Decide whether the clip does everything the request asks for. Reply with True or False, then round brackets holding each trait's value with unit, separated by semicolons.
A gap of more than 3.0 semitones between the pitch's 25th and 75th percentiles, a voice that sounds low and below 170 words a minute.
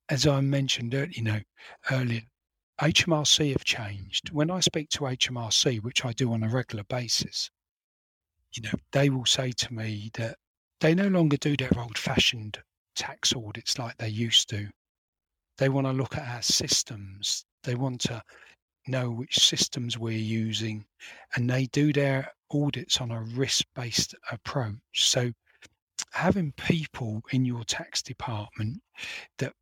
True (3.8 semitones; 125 Hz; 150 wpm)